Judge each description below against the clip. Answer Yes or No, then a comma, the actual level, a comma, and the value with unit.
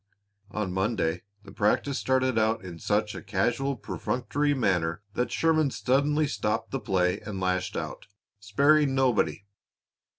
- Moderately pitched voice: No, low, 110 Hz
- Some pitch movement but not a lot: No, wide, 5.7 semitones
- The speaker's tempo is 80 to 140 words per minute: Yes, slow, 135 wpm